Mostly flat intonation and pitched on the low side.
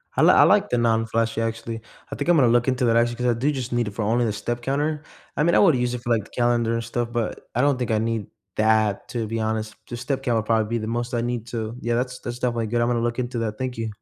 Yes: narrow, 1.6 semitones; low, 120 Hz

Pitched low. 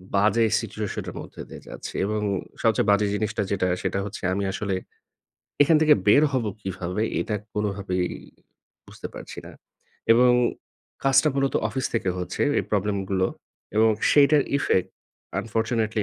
Yes: low, 105 Hz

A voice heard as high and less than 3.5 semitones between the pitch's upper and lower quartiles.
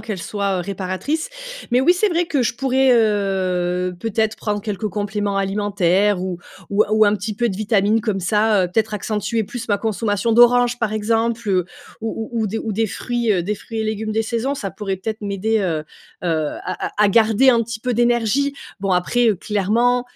Yes: high, 215 Hz; average, 2.8 semitones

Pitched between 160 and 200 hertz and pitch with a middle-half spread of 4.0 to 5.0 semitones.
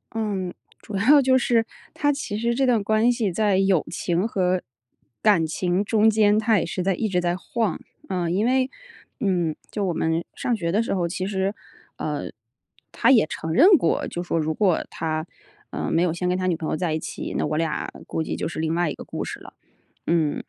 Yes: medium, 185 Hz; average, 4.3 semitones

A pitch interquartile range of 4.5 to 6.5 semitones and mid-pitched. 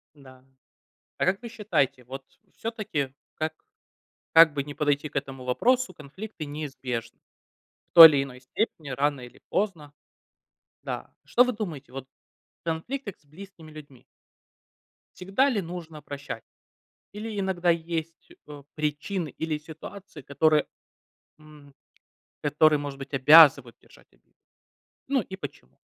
Yes: average, 4.8 semitones; medium, 155 Hz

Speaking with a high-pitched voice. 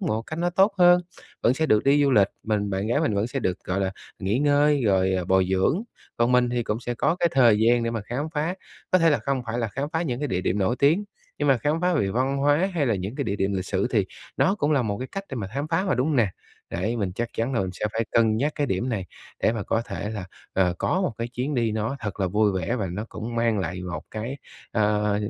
No: low, 115 Hz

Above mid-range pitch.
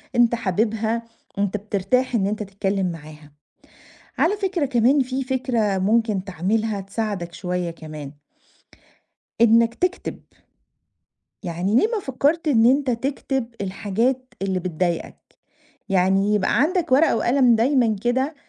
Yes: high, 225 Hz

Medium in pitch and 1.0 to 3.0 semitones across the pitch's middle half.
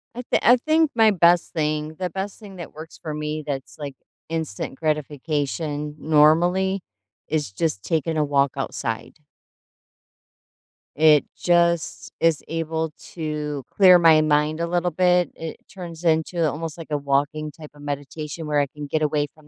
Yes: medium, 155 Hz; narrow, 2.4 semitones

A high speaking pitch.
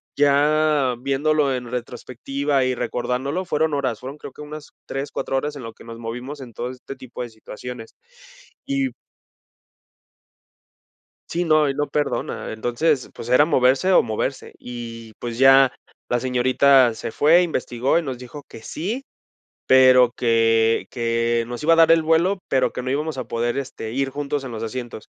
No: low, 130 Hz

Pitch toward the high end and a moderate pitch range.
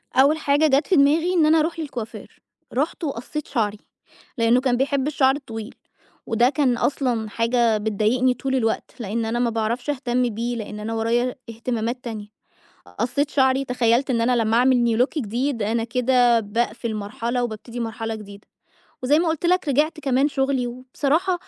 Yes: high, 245 Hz; average, 3.4 semitones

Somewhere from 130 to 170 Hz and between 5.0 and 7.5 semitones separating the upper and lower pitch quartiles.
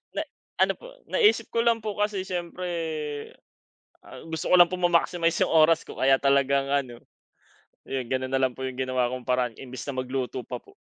Yes: medium, 140 Hz; wide, 5.5 semitones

